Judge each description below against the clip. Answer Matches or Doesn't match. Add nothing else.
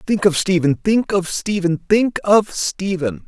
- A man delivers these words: Matches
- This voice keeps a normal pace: Matches